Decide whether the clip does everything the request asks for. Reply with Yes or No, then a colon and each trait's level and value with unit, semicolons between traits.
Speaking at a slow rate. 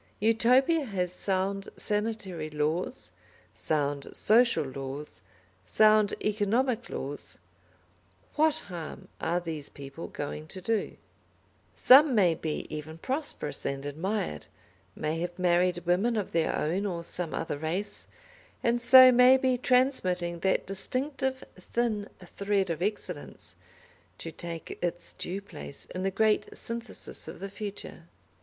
Yes: slow, 125 wpm